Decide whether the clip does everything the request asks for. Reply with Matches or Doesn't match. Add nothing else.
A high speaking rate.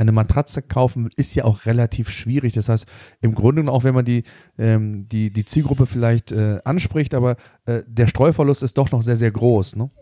Matches